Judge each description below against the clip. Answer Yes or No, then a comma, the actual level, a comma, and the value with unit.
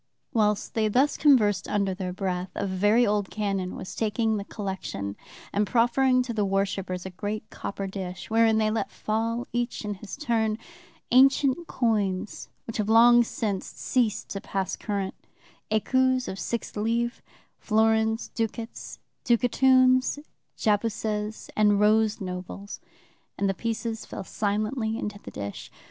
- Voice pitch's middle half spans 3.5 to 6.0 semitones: No, average, 2.8 semitones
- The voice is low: No, high, 215 Hz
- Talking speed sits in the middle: Yes, average, 145 wpm